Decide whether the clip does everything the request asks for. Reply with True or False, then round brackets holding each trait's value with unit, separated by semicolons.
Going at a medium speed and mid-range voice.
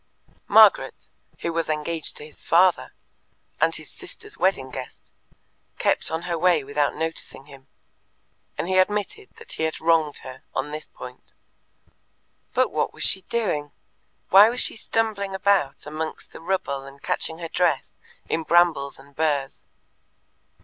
True (150 wpm; 160 Hz)